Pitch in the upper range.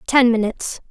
Yes: high, 235 Hz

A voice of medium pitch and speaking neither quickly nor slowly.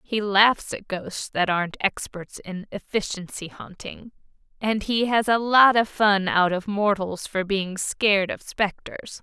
No: high, 200 Hz; average, 165 wpm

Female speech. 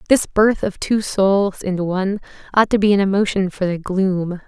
Yes: female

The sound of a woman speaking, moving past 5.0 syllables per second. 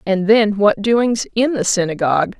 No: female; 4.6 syllables/s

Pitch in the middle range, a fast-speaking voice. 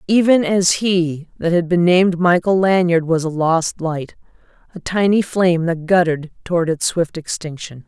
No: medium, 175 Hz; average, 170 wpm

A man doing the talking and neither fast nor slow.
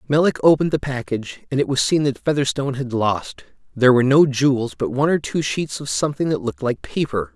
No: male; fast, 220 wpm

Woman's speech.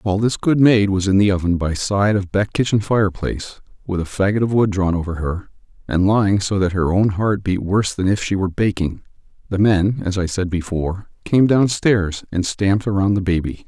No: male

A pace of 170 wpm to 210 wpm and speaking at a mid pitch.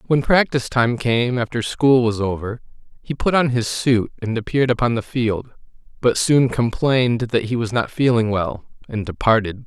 No: average, 180 wpm; low, 120 Hz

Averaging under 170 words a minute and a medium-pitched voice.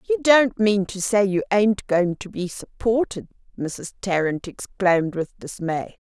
No: average, 160 wpm; high, 200 Hz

